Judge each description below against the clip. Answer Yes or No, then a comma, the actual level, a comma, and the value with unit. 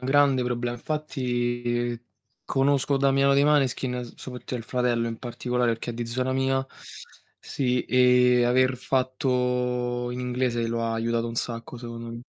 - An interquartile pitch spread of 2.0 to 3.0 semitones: No, narrow, 1.4 semitones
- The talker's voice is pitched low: Yes, low, 125 Hz